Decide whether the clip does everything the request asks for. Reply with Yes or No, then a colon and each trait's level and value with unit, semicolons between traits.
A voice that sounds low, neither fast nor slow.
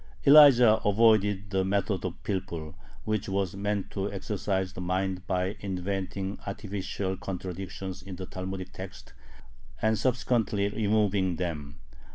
No: very low, 95 Hz; slow, 125 wpm